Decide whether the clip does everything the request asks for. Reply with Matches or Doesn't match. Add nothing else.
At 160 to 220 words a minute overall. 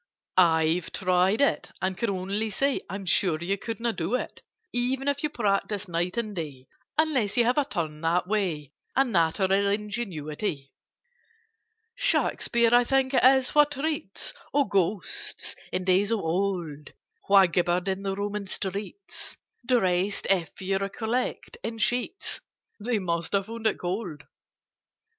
Doesn't match